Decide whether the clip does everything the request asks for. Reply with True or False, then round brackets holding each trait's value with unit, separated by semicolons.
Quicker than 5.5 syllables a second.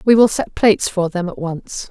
False (5.0 syllables/s)